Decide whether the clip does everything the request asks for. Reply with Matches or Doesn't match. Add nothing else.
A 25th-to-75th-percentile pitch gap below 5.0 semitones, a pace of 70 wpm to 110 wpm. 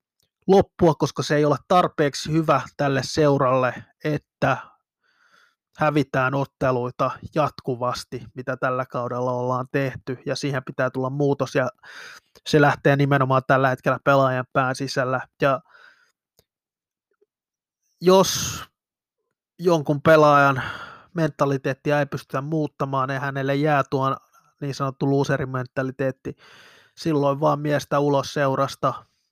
Matches